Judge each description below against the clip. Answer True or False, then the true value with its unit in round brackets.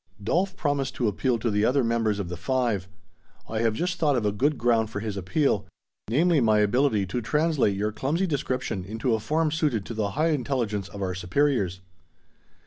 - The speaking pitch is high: False (115 Hz)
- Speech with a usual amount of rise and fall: False (5.7 semitones)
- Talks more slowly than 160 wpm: False (195 wpm)